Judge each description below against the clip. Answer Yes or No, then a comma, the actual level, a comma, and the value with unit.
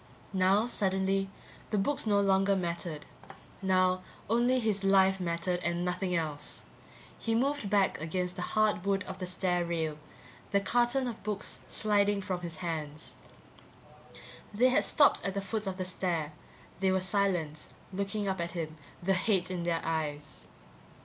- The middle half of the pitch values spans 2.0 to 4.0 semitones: Yes, average, 2.7 semitones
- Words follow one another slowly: No, average, 155 wpm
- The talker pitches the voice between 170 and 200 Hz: Yes, high, 190 Hz